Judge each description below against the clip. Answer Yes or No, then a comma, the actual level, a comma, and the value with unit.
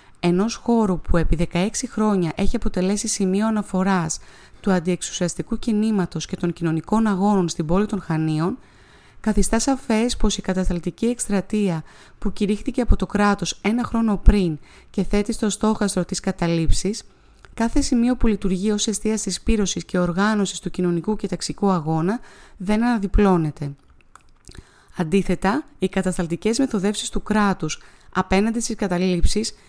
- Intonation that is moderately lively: Yes, average, 3.2 semitones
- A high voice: Yes, high, 200 Hz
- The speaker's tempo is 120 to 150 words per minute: Yes, average, 135 wpm